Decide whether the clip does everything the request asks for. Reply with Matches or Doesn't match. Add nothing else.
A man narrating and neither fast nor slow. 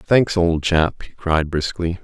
Matches